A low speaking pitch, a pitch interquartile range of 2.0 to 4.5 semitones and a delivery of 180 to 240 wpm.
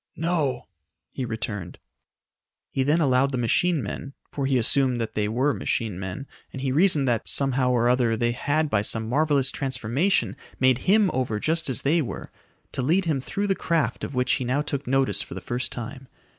Yes: low, 130 Hz; average, 3.5 semitones; average, 195 wpm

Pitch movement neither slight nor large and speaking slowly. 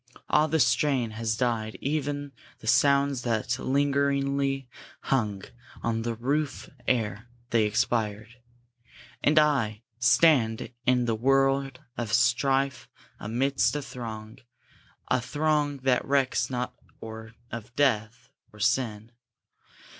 Yes: average, 3.6 semitones; slow, 115 wpm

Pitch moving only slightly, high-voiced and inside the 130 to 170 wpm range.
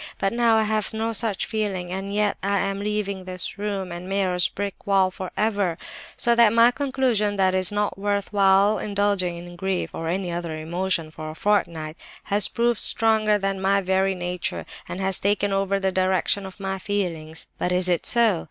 No: narrow, 2.2 semitones; high, 195 Hz; average, 195 wpm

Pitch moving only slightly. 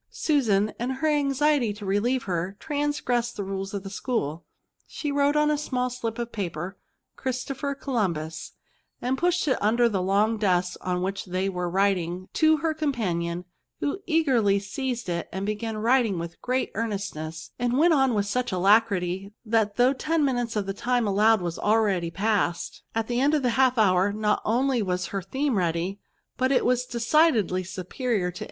No: average, 5.3 semitones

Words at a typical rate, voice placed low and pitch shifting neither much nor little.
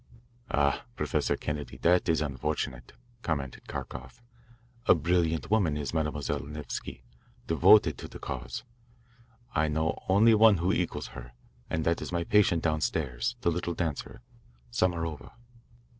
No: slow, 130 wpm; very low, 80 Hz; average, 3.2 semitones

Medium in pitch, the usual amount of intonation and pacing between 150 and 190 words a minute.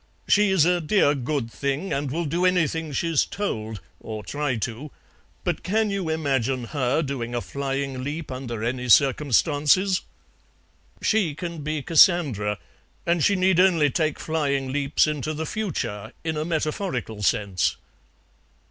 No: medium, 145 Hz; average, 4.7 semitones; average, 140 wpm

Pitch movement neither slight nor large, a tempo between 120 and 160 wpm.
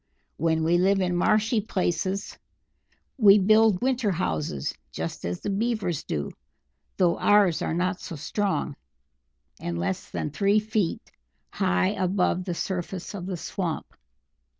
Yes: average, 4.0 semitones; slow, 135 wpm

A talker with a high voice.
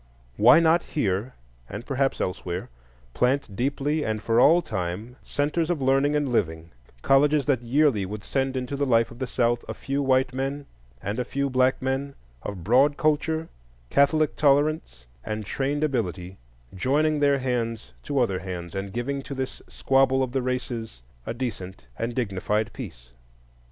No: low, 130 Hz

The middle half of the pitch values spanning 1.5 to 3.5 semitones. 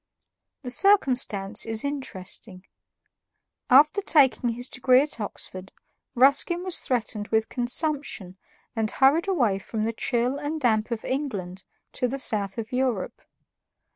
No: average, 4.4 semitones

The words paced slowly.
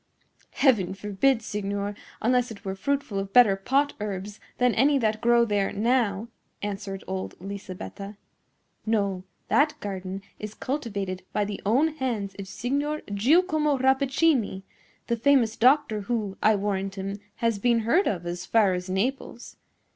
No: average, 145 wpm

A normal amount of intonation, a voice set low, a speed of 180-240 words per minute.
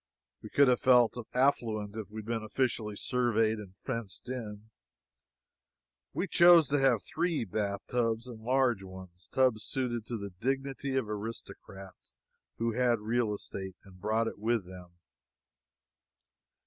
No: average, 3.4 semitones; low, 115 Hz; average, 140 wpm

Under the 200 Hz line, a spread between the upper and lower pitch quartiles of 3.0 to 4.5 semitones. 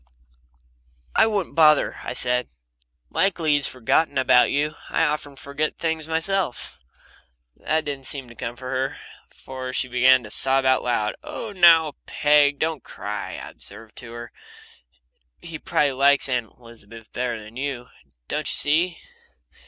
Yes: low, 135 Hz; average, 3.9 semitones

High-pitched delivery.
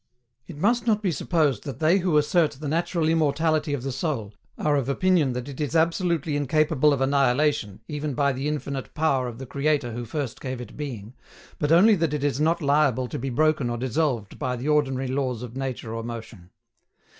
No: medium, 145 Hz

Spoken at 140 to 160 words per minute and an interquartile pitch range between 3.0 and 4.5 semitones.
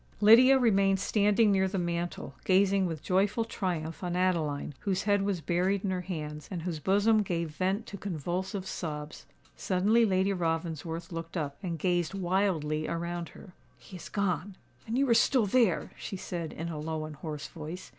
No: average, 175 wpm; average, 3.3 semitones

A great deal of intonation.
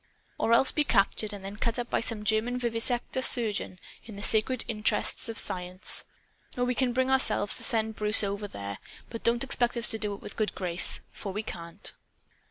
No: average, 2.9 semitones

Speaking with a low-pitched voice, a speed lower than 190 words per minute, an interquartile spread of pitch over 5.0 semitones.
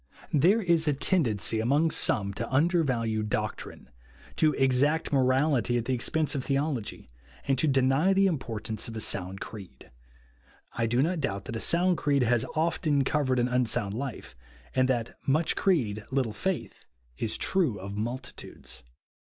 Yes: low, 130 Hz; average, 170 wpm; wide, 5.6 semitones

